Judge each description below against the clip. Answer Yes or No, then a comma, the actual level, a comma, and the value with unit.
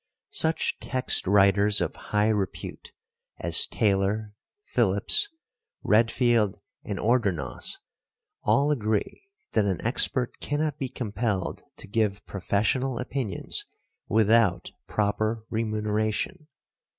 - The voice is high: No, low, 110 Hz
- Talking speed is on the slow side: Yes, slow, 95 wpm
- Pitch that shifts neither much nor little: Yes, average, 3.5 semitones